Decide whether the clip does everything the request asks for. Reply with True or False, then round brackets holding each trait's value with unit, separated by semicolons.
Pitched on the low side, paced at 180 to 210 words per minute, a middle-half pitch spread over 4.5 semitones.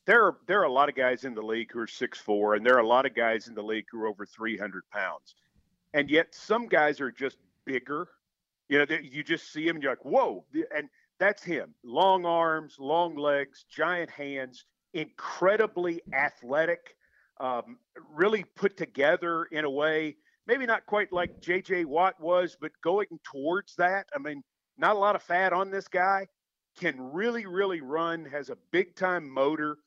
False (165 Hz; 190 wpm; 5.0 semitones)